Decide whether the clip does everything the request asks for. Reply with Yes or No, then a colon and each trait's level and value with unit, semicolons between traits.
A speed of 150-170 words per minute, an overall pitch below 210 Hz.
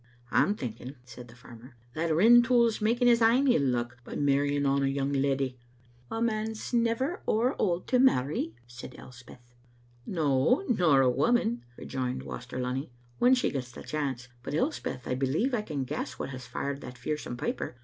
No: average, 180 wpm; medium, 140 Hz